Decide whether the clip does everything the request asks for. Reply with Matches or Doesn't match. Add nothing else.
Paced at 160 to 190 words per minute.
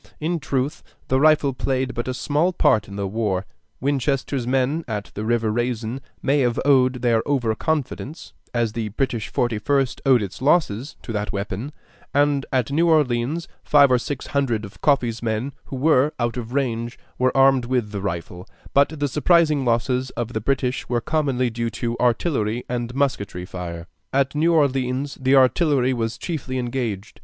Matches